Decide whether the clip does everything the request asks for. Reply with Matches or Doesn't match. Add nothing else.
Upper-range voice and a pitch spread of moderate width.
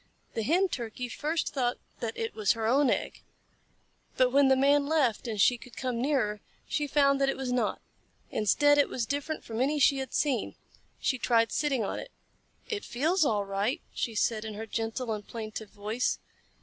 Matches